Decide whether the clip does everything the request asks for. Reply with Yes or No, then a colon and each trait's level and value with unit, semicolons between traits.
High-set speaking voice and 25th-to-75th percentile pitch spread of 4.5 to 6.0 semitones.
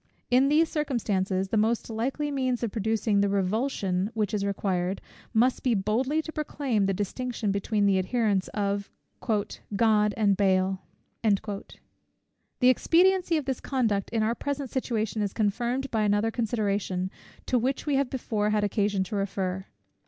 No: high, 215 Hz; average, 4.0 semitones